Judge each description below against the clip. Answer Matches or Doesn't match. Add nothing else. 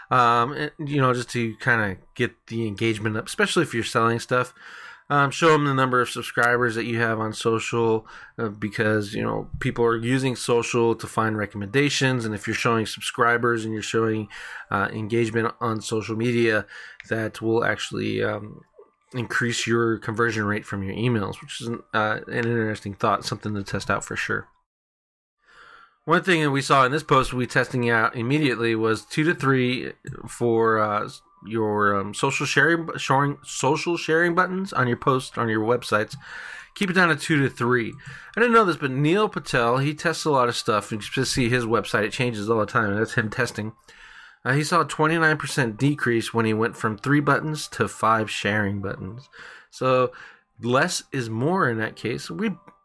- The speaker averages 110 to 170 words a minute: Doesn't match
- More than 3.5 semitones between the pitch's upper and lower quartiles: Matches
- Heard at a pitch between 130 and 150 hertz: Doesn't match